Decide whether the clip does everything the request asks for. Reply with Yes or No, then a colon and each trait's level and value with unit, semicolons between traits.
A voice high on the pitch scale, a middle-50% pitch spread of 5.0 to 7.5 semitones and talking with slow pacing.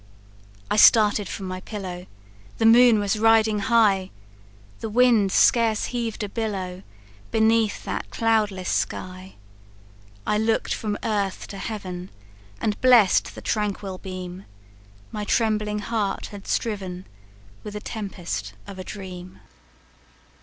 No: high, 210 Hz; average, 2.8 semitones; slow, 125 wpm